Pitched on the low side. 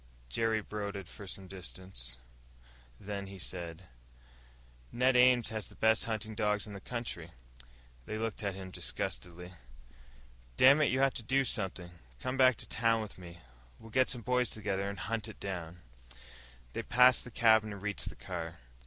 Yes: low, 105 Hz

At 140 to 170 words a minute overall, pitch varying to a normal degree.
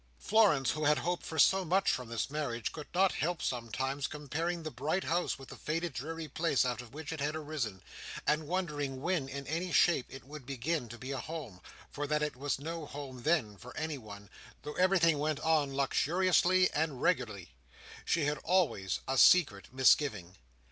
No: average, 185 wpm; average, 4.0 semitones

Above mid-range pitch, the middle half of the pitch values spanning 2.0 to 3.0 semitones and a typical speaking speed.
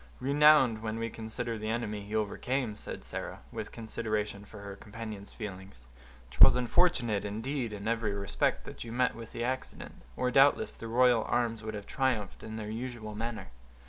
No: low, 110 Hz; narrow, 2.5 semitones; average, 175 wpm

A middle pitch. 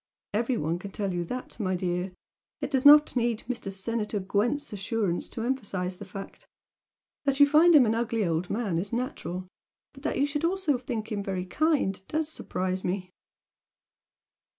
No: high, 215 Hz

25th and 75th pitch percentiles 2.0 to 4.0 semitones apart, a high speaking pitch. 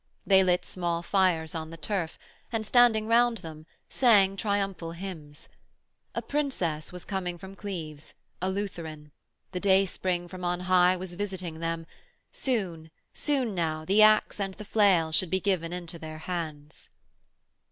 No: average, 3.3 semitones; medium, 180 Hz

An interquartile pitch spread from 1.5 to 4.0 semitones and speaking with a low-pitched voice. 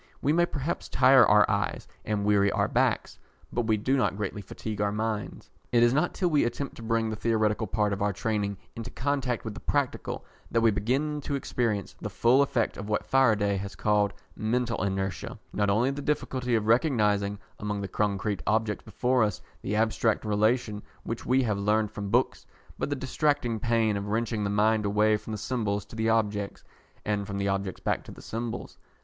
Yes: average, 3.0 semitones; low, 110 Hz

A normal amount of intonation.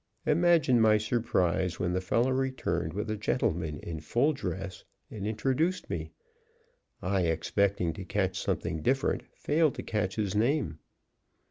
No: wide, 6.2 semitones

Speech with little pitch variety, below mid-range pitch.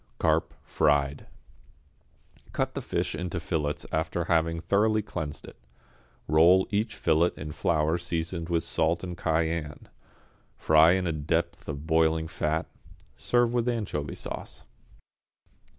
Yes: narrow, 2.1 semitones; very low, 80 Hz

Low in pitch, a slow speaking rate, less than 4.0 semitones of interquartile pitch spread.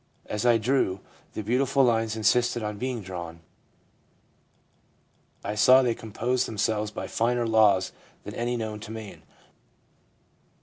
Yes: low, 110 Hz; slow, 130 wpm; narrow, 2.4 semitones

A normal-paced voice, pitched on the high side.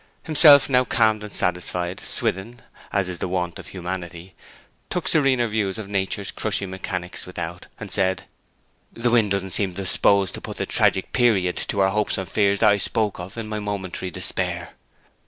No: average, 175 wpm; low, 100 Hz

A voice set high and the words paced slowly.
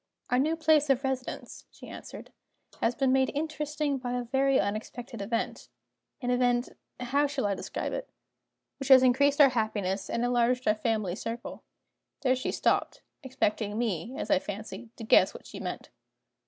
No: very high, 250 Hz; average, 165 wpm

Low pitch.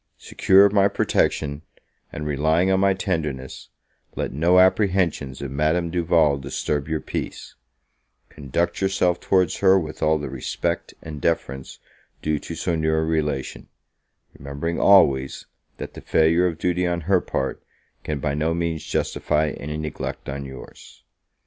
Yes: very low, 80 Hz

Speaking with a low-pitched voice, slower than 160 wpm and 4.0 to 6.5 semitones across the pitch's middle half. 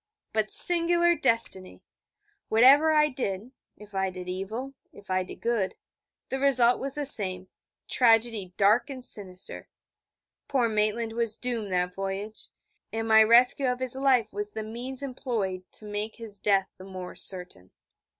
No: high, 220 Hz; average, 150 wpm; average, 4.6 semitones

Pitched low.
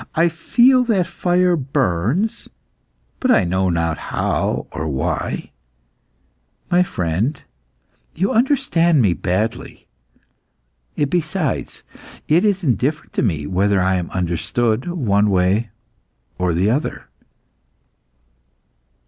Yes: low, 120 Hz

